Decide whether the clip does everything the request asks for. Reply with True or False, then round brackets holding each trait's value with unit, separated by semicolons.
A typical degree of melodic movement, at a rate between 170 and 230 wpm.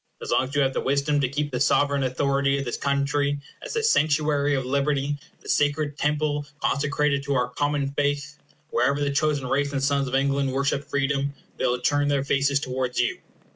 False (1.0 semitones; 200 wpm)